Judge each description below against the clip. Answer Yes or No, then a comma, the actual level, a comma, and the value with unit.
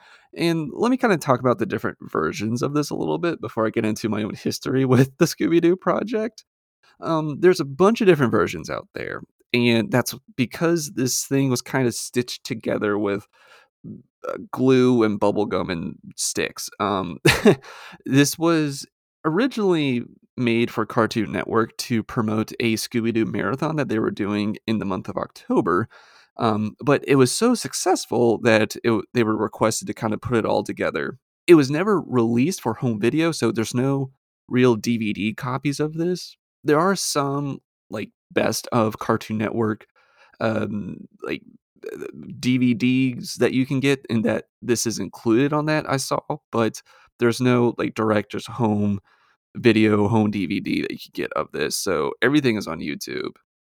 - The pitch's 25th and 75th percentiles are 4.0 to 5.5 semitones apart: Yes, average, 4.6 semitones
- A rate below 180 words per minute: Yes, average, 165 wpm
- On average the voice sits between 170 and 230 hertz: No, low, 125 Hz